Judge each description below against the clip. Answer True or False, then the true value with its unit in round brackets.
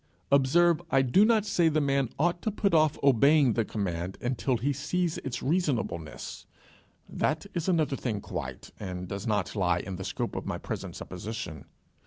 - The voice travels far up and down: True (7.9 semitones)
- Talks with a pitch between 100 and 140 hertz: True (135 Hz)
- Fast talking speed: False (175 wpm)